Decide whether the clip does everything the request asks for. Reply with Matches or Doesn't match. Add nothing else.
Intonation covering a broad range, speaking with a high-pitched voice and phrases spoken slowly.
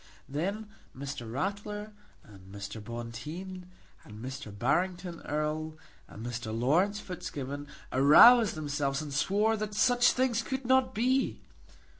Doesn't match